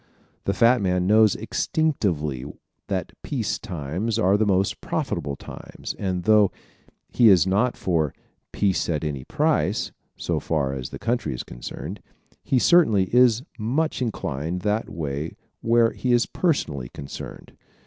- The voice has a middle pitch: No, low, 100 Hz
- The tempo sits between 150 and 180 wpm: No, average, 140 wpm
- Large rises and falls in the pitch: Yes, wide, 7.1 semitones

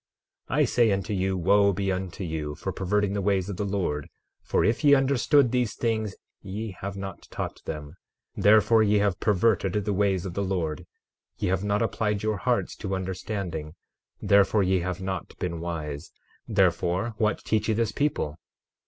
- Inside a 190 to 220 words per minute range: No, average, 180 wpm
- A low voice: Yes, low, 100 Hz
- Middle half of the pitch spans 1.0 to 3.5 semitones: Yes, average, 2.8 semitones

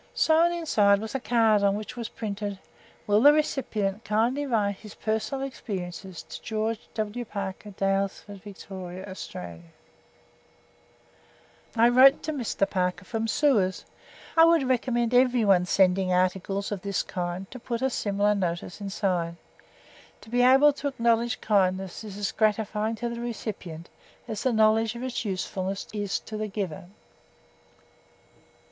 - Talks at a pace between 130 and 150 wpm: Yes, average, 140 wpm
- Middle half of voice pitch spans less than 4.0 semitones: Yes, average, 3.6 semitones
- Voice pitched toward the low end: No, high, 210 Hz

